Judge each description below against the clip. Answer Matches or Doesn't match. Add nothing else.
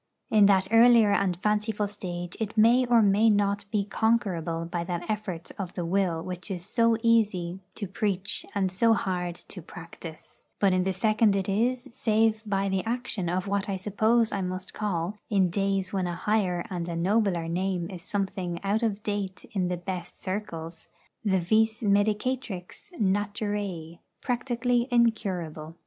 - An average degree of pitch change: Matches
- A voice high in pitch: Matches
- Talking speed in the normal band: Matches